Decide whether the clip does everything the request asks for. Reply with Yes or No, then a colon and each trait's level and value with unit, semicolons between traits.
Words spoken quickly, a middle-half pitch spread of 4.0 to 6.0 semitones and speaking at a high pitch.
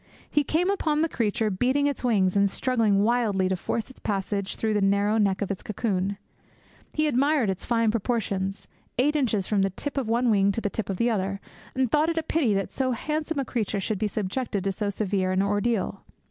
Yes: fast, 215 wpm; average, 4.5 semitones; high, 215 Hz